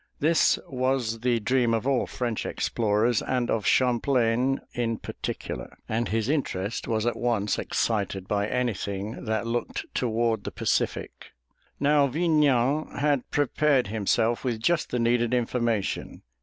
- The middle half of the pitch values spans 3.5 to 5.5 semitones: No, average, 2.8 semitones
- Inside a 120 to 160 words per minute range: Yes, slow, 135 wpm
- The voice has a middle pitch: No, low, 120 Hz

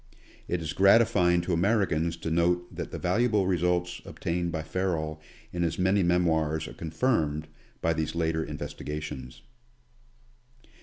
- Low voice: Yes, very low, 85 Hz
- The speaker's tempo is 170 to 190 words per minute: No, average, 140 wpm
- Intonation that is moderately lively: No, narrow, 2.3 semitones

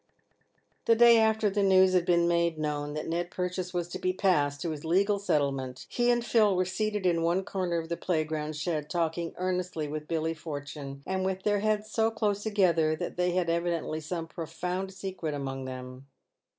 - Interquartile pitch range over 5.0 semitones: No, average, 3.5 semitones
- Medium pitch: Yes, medium, 175 Hz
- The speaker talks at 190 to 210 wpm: Yes, average, 195 wpm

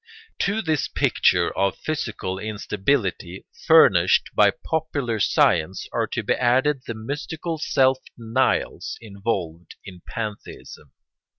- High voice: No, low, 115 Hz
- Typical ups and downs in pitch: No, wide, 6.9 semitones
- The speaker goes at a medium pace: No, slow, 115 wpm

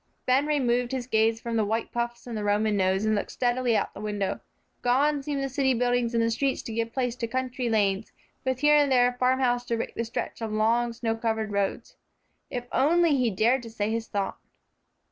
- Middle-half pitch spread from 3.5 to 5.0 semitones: No, narrow, 2.6 semitones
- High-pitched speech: Yes, high, 235 Hz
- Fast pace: Yes, fast, 220 wpm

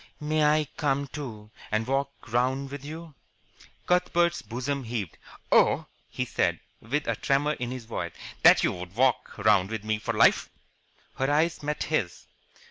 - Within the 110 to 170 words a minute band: Yes, average, 160 wpm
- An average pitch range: Yes, average, 5.0 semitones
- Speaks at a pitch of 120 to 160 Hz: Yes, low, 135 Hz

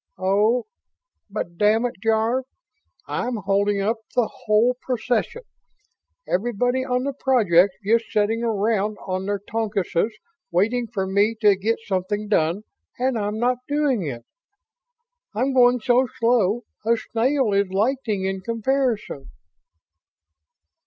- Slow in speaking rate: Yes, slow, 125 wpm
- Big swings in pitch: No, average, 3.6 semitones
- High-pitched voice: Yes, high, 220 Hz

